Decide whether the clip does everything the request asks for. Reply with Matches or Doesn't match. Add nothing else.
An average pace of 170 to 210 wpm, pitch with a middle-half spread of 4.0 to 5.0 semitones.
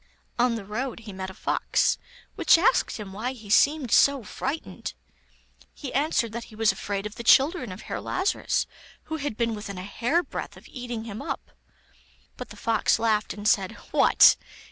Matches